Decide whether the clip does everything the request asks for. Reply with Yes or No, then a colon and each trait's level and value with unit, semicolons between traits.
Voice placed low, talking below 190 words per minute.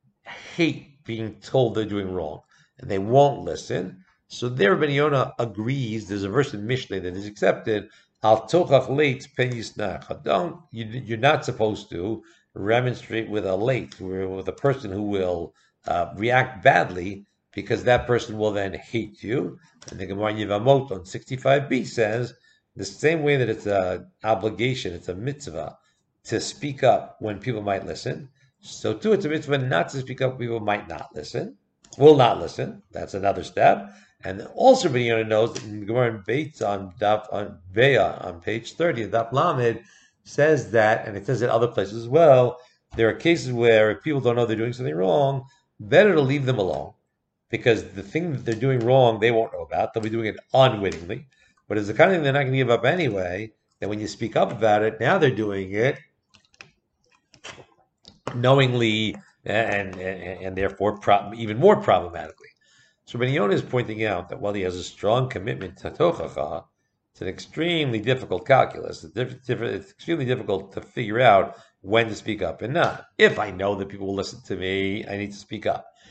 Yes: low, 115 Hz; average, 180 wpm